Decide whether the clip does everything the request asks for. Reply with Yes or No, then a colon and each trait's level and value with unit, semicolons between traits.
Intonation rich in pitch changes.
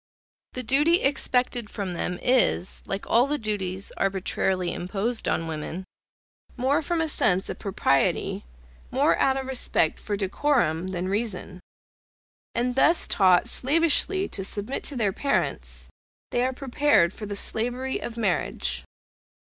Yes: wide, 5.9 semitones